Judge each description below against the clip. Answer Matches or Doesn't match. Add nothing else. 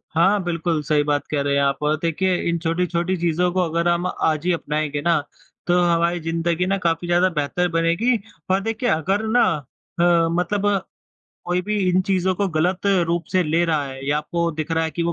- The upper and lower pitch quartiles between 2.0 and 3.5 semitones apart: Matches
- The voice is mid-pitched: Matches